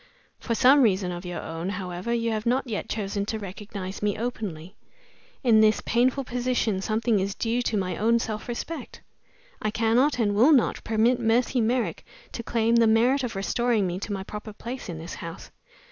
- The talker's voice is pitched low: No, high, 220 Hz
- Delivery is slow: No, average, 190 wpm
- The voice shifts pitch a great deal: No, average, 3.2 semitones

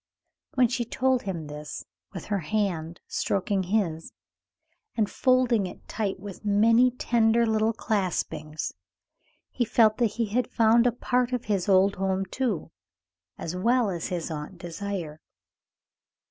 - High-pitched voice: Yes, high, 205 Hz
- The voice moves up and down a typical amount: Yes, average, 4.3 semitones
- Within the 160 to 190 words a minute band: No, slow, 135 wpm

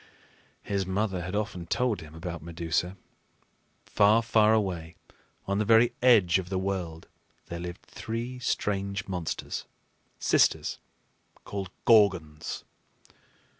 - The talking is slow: Yes, slow, 115 wpm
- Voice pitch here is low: Yes, very low, 95 Hz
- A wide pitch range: No, average, 3.7 semitones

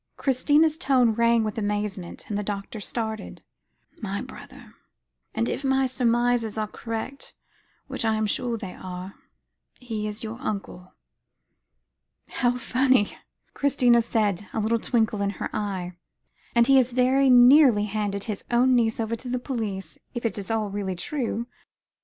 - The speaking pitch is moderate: No, high, 225 Hz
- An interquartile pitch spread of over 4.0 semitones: No, average, 3.2 semitones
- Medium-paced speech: Yes, average, 150 wpm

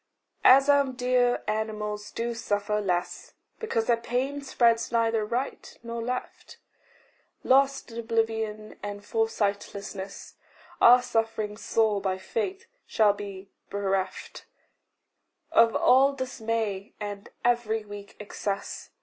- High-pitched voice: Yes, high, 225 Hz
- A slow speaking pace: Yes, slow, 110 wpm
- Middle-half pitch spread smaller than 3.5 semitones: Yes, average, 3.0 semitones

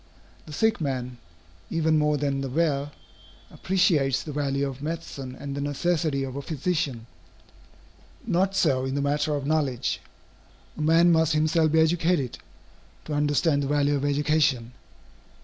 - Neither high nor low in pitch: Yes, medium, 145 Hz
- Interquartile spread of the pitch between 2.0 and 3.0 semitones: Yes, average, 2.7 semitones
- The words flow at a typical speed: Yes, average, 150 wpm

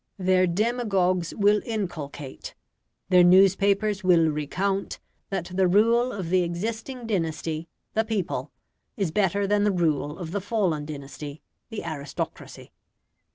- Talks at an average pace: No, slow, 125 wpm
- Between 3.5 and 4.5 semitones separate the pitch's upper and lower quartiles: Yes, average, 4.0 semitones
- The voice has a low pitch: No, medium, 185 Hz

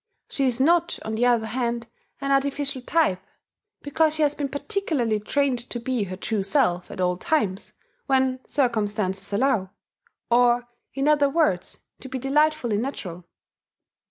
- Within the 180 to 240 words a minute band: No, average, 150 wpm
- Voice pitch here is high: Yes, very high, 250 Hz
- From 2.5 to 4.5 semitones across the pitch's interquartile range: No, average, 5.0 semitones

